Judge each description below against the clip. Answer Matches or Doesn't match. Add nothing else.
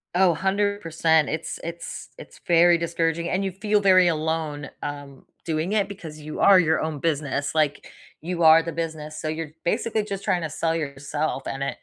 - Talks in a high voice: Doesn't match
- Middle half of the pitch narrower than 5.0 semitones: Matches